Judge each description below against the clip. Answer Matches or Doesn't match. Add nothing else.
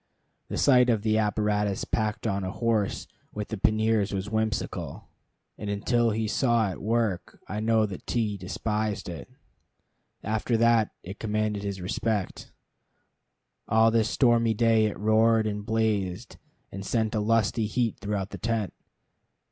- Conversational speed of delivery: Matches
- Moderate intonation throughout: Doesn't match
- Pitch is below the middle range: Matches